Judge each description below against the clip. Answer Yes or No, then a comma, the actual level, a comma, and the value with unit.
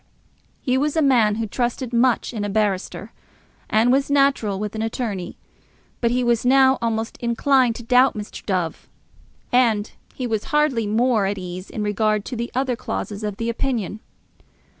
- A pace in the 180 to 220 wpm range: No, average, 170 wpm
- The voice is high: Yes, high, 230 Hz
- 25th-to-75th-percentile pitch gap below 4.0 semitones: Yes, average, 3.4 semitones